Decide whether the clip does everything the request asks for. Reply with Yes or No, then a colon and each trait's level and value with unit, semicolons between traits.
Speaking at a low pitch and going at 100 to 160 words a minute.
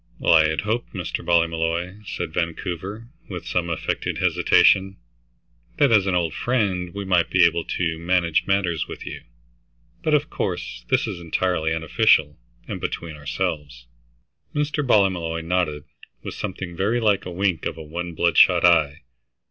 Yes: very low, 85 Hz; average, 150 wpm